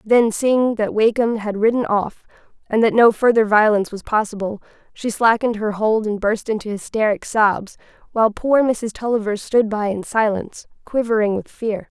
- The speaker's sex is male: No, female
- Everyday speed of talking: Yes, average, 170 wpm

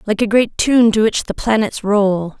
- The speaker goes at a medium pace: No, fast, 225 wpm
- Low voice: No, high, 215 Hz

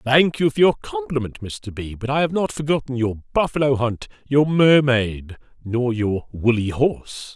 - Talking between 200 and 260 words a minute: No, average, 170 wpm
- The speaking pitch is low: Yes, low, 125 Hz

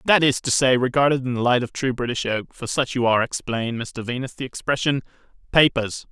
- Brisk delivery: Yes, fast, 215 wpm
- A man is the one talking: Yes, male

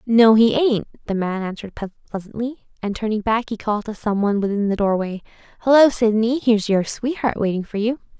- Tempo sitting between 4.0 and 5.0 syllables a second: No, 5.6 syllables/s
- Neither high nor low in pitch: No, high, 220 Hz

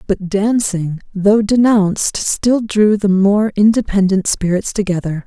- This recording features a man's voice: No, female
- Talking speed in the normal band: No, slow, 125 wpm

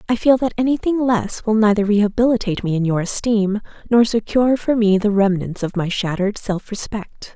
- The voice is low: No, high, 215 Hz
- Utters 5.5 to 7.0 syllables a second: Yes, 5.6 syllables/s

